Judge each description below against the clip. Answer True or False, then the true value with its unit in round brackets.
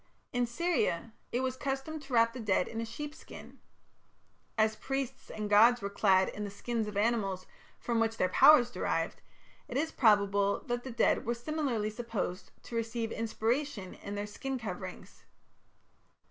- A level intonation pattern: False (3.7 semitones)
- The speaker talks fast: False (170 wpm)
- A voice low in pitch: False (230 Hz)